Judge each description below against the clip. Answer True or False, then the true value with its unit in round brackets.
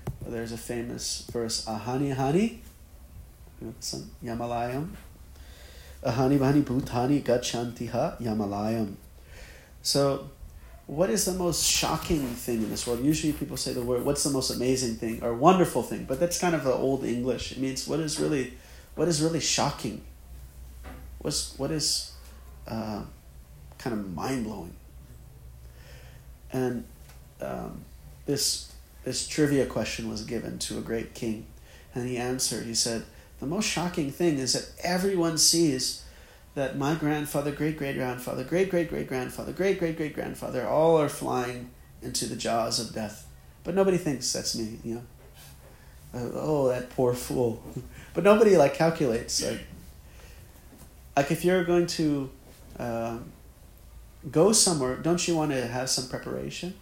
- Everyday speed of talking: True (145 wpm)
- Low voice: True (125 Hz)